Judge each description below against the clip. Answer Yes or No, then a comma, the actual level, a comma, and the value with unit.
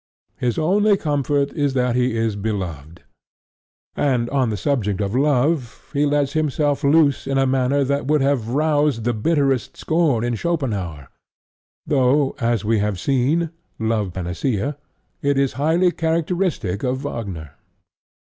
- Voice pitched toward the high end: No, low, 135 Hz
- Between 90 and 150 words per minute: Yes, average, 140 wpm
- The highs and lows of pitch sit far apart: No, average, 4.6 semitones